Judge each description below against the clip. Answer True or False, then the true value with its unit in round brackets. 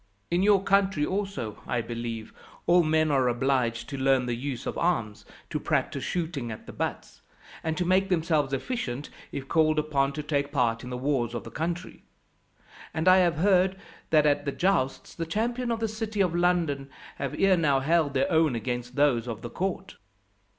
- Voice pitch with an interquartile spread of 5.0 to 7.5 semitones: True (5.5 semitones)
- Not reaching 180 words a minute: False (190 wpm)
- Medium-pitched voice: True (150 Hz)